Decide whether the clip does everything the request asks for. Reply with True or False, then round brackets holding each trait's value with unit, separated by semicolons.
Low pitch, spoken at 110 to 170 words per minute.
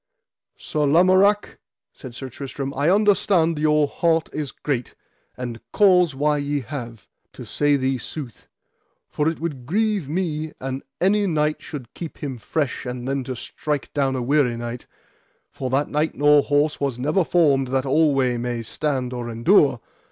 False (145 Hz; 160 wpm)